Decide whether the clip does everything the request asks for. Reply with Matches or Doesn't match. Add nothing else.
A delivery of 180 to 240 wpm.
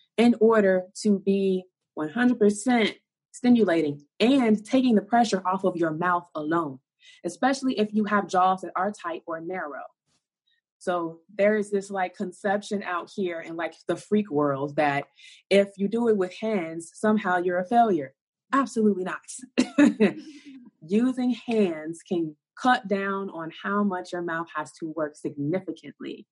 Doesn't match